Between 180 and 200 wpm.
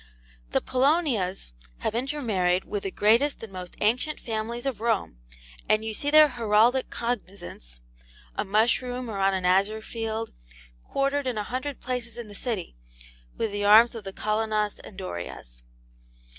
No: average, 155 wpm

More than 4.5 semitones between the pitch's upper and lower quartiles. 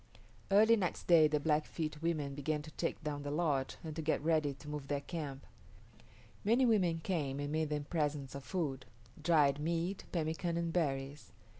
No: average, 2.8 semitones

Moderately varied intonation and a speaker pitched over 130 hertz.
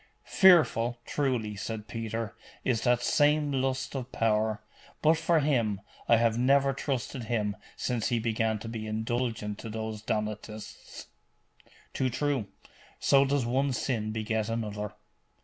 No: average, 3.5 semitones; low, 115 Hz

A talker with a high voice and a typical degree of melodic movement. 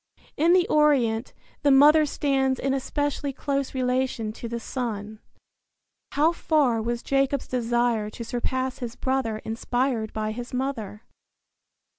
Yes: very high, 255 Hz; average, 3.3 semitones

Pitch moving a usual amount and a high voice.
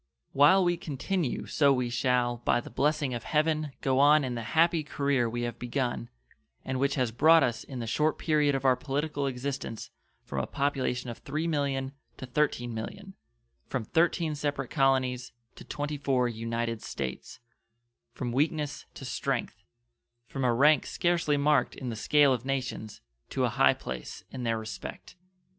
No: average, 3.5 semitones; low, 135 Hz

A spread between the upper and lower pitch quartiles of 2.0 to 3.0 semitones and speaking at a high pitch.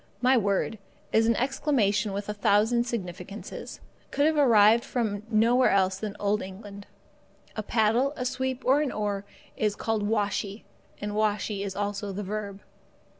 Yes: average, 2.7 semitones; high, 210 Hz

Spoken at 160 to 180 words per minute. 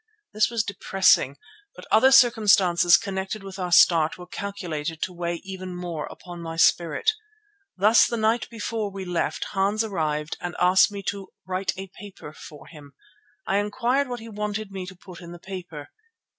Yes: average, 170 wpm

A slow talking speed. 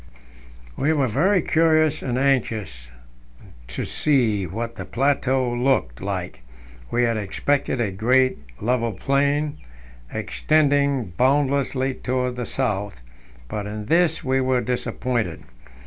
Yes: slow, 115 wpm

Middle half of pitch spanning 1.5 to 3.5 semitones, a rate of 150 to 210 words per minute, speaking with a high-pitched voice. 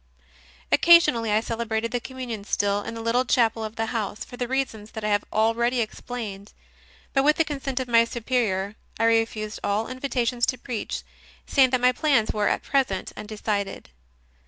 Yes: average, 2.9 semitones; average, 180 wpm; high, 230 Hz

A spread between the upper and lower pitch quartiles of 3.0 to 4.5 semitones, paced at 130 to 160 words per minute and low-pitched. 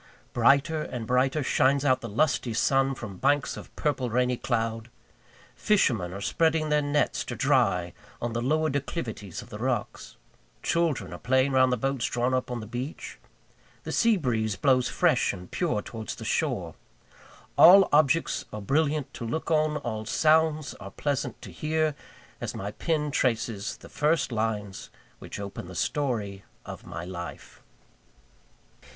No: average, 5.3 semitones; average, 155 wpm; low, 130 Hz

